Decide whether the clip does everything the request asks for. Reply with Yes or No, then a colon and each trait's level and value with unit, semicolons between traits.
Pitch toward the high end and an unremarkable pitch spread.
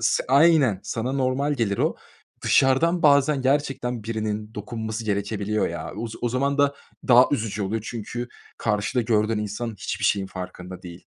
No: low, 115 Hz; average, 4.2 semitones